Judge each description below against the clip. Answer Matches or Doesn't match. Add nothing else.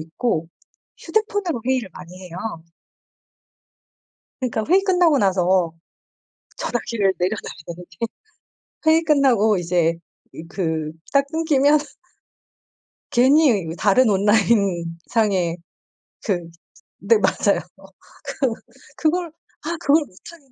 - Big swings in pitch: Matches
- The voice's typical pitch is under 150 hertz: Doesn't match